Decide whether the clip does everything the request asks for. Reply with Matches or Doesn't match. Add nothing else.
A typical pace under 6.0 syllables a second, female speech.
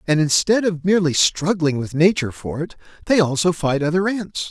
Doesn't match